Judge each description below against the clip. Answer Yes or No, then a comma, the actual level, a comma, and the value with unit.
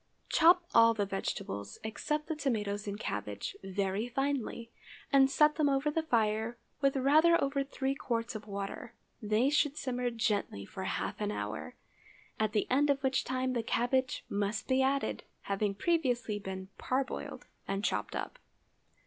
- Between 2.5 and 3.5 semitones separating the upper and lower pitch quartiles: No, average, 5.0 semitones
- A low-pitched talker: No, high, 240 Hz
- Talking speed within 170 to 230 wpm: No, average, 155 wpm